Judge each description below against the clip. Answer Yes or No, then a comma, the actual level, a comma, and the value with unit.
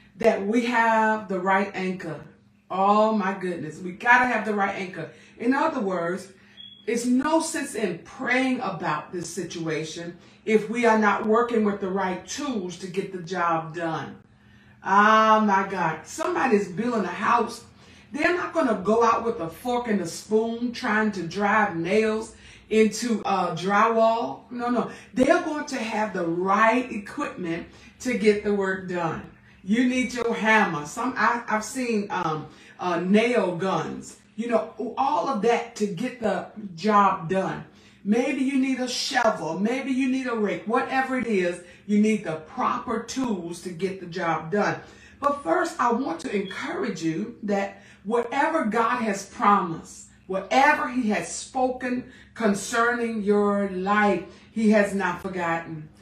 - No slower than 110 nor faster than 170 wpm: Yes, average, 155 wpm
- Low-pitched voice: No, high, 215 Hz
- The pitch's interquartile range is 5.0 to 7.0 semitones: No, average, 4.2 semitones